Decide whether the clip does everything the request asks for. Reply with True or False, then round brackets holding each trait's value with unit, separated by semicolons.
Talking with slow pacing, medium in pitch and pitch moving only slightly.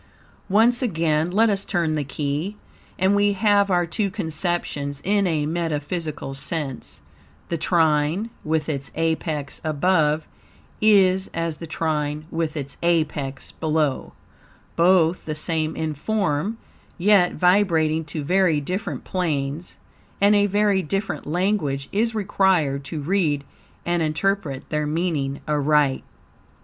False (125 wpm; 165 Hz; 4.1 semitones)